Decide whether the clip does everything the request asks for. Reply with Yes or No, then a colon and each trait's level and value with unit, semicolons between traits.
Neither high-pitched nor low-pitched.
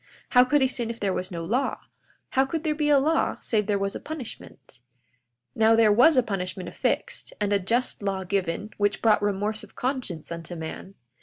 No: high, 210 Hz